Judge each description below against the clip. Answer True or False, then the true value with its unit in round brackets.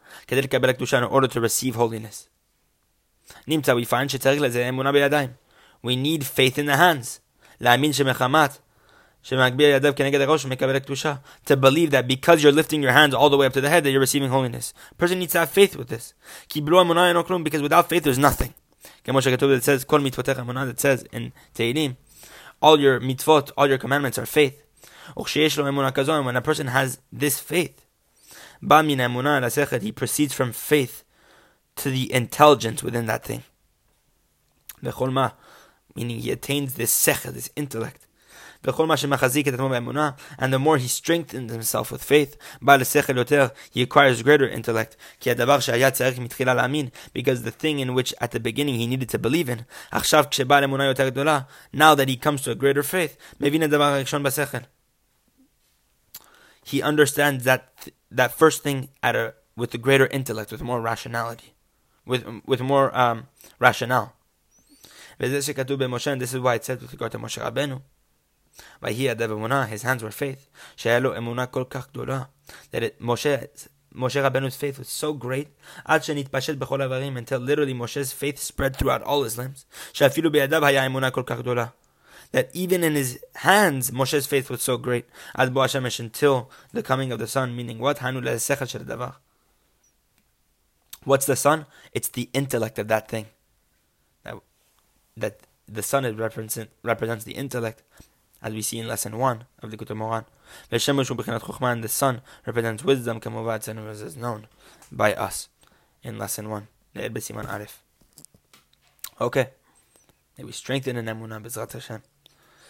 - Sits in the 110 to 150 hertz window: True (135 Hz)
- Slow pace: True (120 wpm)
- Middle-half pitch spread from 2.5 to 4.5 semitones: True (3.0 semitones)